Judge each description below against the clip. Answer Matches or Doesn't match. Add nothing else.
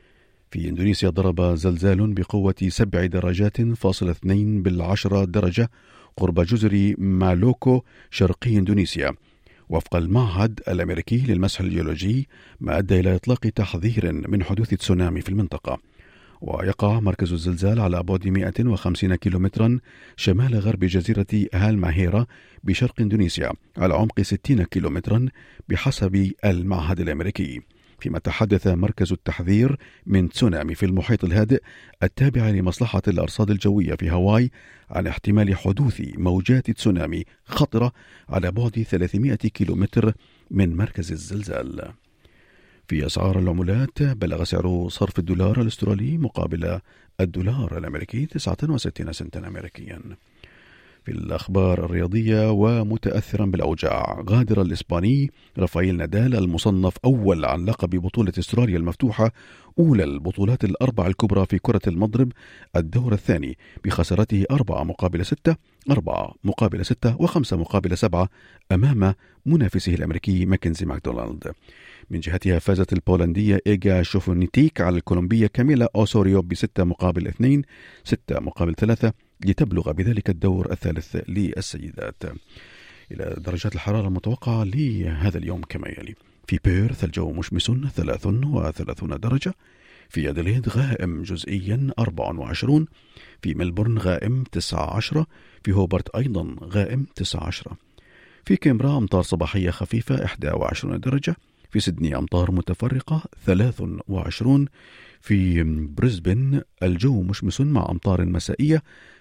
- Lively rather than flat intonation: Doesn't match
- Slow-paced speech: Doesn't match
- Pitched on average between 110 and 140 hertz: Doesn't match